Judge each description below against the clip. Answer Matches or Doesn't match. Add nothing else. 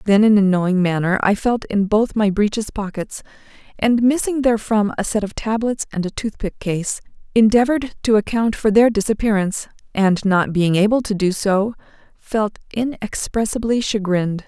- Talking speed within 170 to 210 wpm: Doesn't match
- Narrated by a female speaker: Matches